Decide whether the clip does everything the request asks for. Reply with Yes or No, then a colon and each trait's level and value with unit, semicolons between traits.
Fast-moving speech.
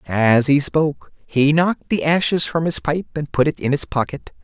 Yes: fast, 215 wpm